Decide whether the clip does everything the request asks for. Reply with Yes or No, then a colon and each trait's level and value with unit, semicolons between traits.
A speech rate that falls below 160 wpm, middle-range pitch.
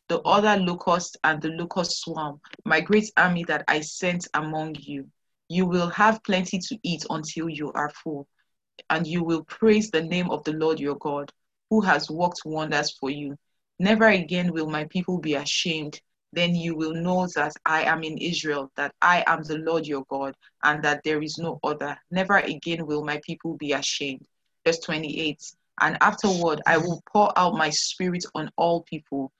No: average, 185 wpm; medium, 160 Hz